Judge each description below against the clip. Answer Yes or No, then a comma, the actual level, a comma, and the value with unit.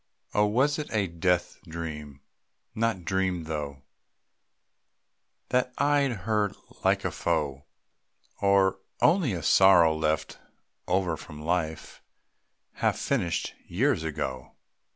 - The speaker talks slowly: Yes, slow, 110 wpm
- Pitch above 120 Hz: No, very low, 90 Hz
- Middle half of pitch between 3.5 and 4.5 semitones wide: No, average, 5.1 semitones